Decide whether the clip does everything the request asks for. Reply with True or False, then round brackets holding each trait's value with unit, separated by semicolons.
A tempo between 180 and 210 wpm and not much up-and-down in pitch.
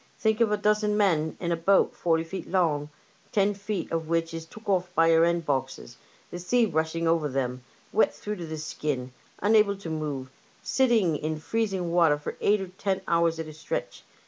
False (200 wpm; 4.2 semitones)